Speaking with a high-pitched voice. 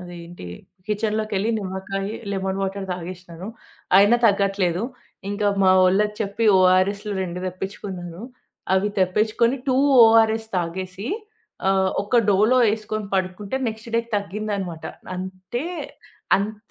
Yes: high, 195 Hz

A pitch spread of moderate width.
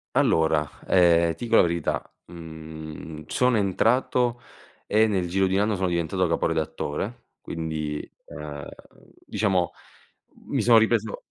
Yes: average, 5.0 semitones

